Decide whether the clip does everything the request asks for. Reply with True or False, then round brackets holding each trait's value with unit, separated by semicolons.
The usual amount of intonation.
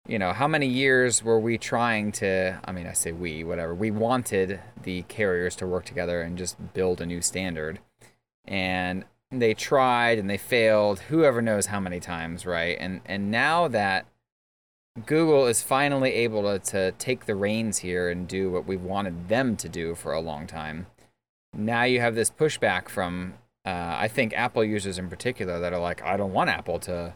True (4.3 semitones)